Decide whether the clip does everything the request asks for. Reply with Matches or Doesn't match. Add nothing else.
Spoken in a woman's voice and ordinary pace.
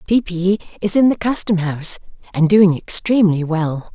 Matches